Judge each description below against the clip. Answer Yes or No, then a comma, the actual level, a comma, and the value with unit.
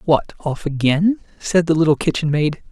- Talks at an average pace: Yes, average, 175 wpm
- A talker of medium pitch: Yes, medium, 160 Hz